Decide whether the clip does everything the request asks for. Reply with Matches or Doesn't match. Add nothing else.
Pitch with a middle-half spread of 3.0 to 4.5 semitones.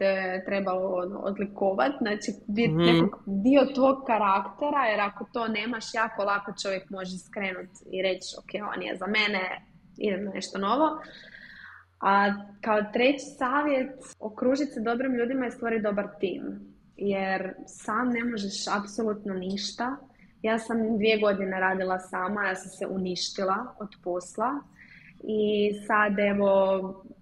Matches